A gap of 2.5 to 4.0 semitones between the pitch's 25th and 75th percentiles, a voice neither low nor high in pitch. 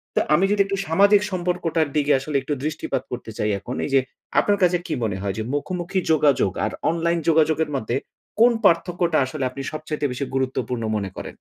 No: average, 4.7 semitones; medium, 155 Hz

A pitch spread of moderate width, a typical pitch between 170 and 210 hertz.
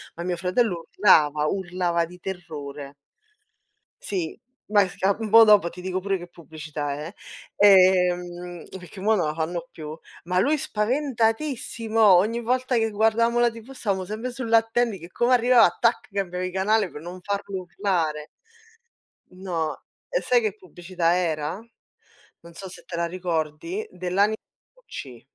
Yes: average, 4.6 semitones; medium, 185 Hz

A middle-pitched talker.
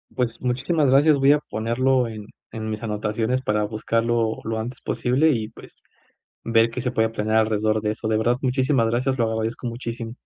No: low, 115 Hz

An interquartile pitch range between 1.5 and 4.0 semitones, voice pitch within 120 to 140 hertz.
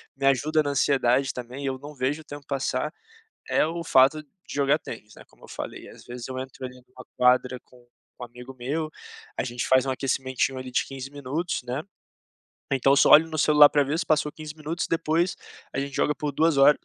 Yes: average, 2.8 semitones; low, 135 Hz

